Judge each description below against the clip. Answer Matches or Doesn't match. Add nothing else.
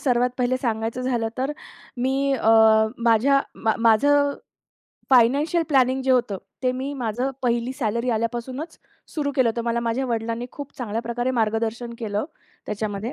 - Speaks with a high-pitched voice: Matches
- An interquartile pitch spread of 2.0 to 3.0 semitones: Matches